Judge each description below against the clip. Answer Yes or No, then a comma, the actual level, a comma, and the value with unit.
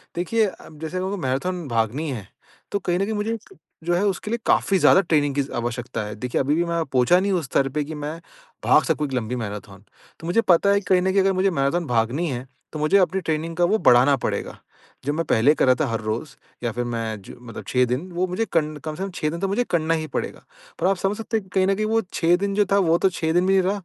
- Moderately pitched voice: Yes, medium, 165 Hz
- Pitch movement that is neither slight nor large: No, wide, 6.5 semitones